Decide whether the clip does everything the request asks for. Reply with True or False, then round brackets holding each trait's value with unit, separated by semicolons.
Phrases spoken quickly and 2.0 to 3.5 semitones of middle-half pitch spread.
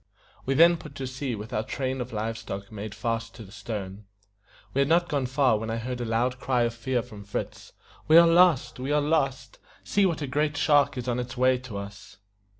False (230 wpm; 4.0 semitones)